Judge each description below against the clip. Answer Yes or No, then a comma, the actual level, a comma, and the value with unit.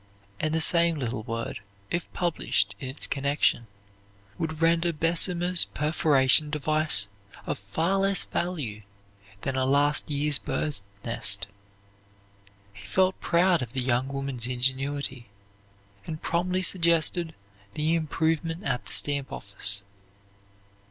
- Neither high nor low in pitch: Yes, medium, 150 Hz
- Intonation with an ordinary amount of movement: Yes, average, 4.6 semitones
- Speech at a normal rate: No, slow, 120 wpm